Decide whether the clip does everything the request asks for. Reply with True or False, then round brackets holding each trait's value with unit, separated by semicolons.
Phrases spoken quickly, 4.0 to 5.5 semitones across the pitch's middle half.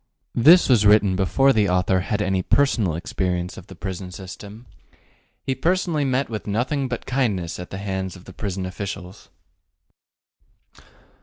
False (150 wpm; 5.0 semitones)